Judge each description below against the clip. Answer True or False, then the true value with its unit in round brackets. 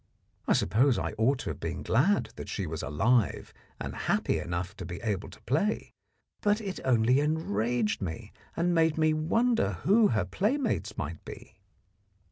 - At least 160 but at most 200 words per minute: True (165 wpm)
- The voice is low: True (120 Hz)